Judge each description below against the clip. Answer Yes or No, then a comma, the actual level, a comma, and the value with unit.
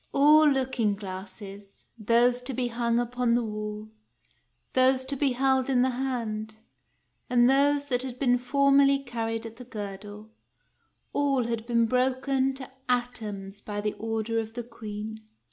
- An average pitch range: Yes, average, 3.2 semitones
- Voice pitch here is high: Yes, high, 240 Hz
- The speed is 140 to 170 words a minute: Yes, average, 160 wpm